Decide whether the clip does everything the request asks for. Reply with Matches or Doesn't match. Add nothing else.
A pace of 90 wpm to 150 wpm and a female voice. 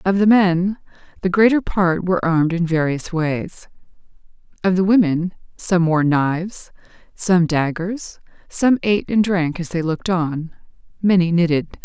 Matches